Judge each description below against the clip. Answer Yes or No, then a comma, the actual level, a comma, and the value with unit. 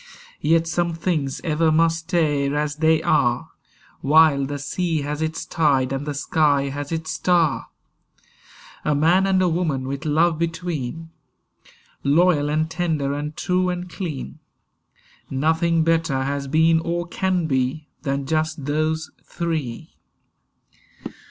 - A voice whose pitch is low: No, medium, 155 Hz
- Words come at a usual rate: No, slow, 130 wpm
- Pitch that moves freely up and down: No, narrow, 2.5 semitones